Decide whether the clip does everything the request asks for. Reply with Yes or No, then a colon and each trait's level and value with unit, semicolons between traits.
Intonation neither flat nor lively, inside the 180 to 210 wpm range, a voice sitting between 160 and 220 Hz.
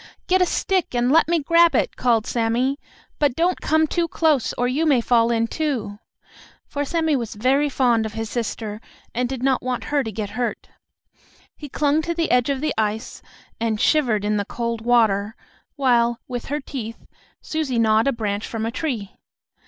No: average, 4.6 semitones; average, 190 wpm; high, 245 Hz